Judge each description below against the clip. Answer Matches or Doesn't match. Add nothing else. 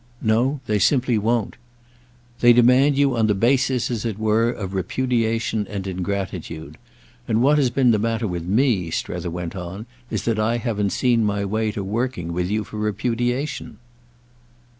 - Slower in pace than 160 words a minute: Doesn't match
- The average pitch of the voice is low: Matches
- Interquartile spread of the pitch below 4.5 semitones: Matches